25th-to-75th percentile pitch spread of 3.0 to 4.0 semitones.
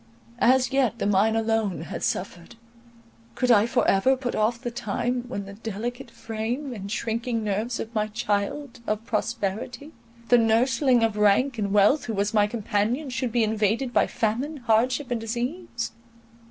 No: narrow, 2.6 semitones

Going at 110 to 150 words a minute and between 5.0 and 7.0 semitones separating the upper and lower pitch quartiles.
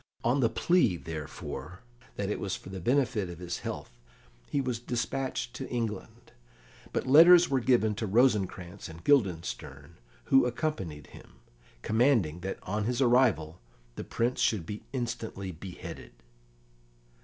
Yes: average, 140 wpm; wide, 5.6 semitones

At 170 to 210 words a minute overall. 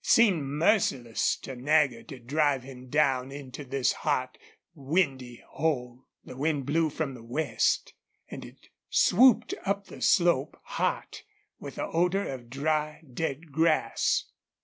No: average, 140 wpm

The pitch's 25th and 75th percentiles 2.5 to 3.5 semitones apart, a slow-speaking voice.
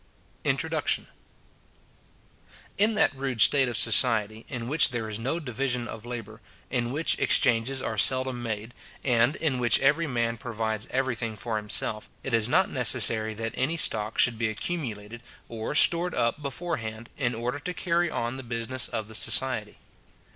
No: average, 3.2 semitones; average, 165 wpm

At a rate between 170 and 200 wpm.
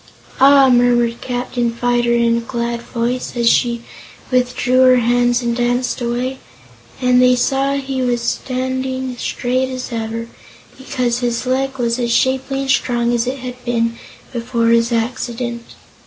No: average, 150 wpm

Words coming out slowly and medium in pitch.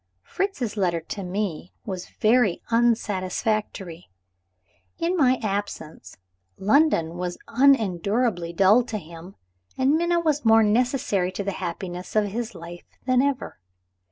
No: slow, 125 wpm; high, 210 Hz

